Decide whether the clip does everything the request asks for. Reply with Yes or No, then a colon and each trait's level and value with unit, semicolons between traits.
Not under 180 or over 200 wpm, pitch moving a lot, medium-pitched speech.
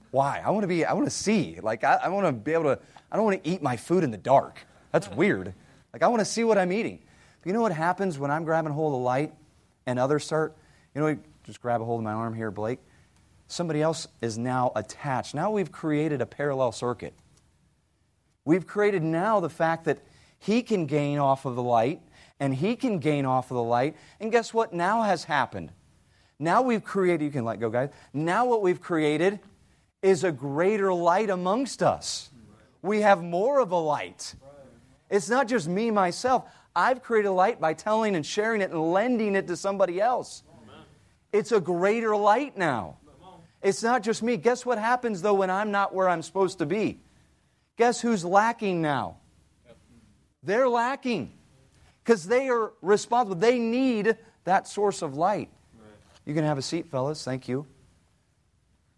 Yes: average, 195 wpm; wide, 7.5 semitones; medium, 170 Hz